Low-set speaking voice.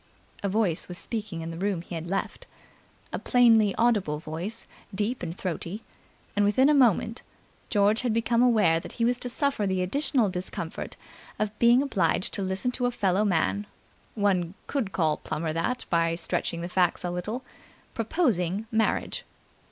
No: high, 205 Hz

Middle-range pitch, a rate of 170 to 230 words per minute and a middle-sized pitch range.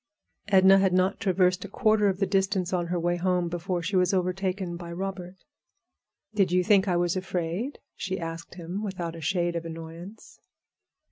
No: medium, 180 Hz; average, 180 wpm; narrow, 1.9 semitones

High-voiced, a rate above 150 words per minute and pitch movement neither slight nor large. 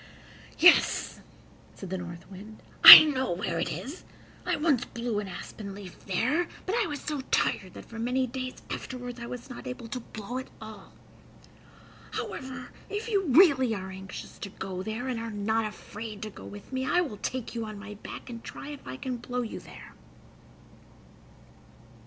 Yes: high, 235 Hz; average, 180 wpm; average, 4.1 semitones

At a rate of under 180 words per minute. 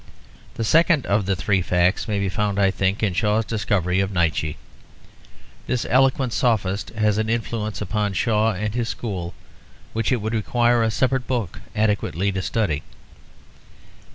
Yes: average, 155 wpm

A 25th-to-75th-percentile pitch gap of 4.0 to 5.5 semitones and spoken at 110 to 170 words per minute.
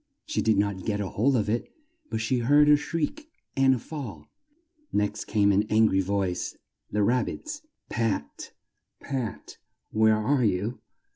Yes: average, 4.7 semitones; average, 155 wpm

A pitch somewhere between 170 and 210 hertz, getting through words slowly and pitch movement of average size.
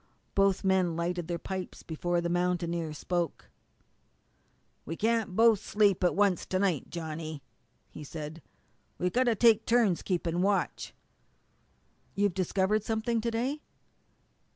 Yes: medium, 185 Hz; slow, 130 wpm; average, 3.8 semitones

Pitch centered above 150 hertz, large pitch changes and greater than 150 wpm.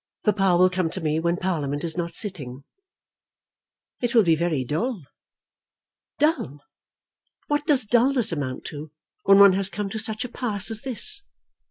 Yes: high, 190 Hz; wide, 5.9 semitones; average, 160 wpm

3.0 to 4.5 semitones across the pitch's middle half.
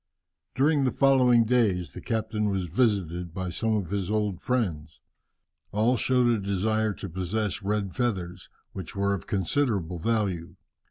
Yes: average, 4.0 semitones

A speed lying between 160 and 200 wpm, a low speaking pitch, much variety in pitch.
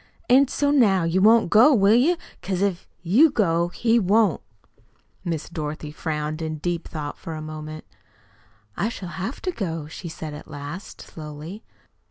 No: average, 165 wpm; medium, 175 Hz; wide, 6.0 semitones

